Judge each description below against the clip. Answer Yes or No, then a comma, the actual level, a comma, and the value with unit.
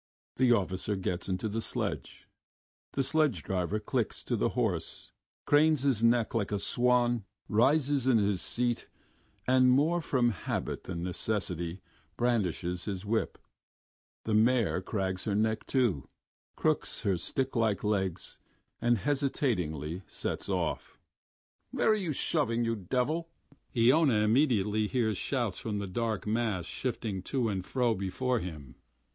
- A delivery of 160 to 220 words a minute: No, average, 140 wpm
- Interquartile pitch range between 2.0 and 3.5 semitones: No, average, 4.8 semitones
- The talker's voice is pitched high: No, low, 110 Hz